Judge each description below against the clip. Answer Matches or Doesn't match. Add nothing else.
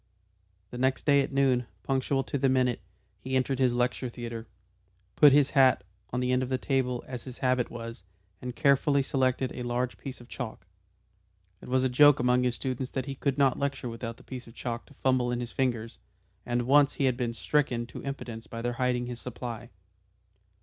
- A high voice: Doesn't match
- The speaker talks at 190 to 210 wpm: Matches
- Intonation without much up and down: Matches